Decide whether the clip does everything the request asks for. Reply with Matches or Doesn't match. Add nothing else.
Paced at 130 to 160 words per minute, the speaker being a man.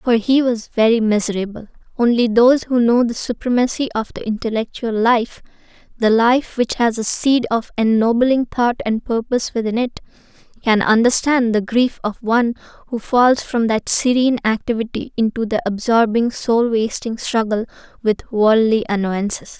Doesn't match